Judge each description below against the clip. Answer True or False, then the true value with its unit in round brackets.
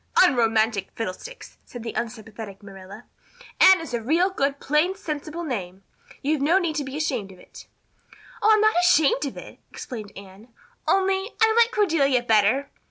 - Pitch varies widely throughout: True (7.8 semitones)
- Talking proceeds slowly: False (165 wpm)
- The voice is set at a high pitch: True (275 Hz)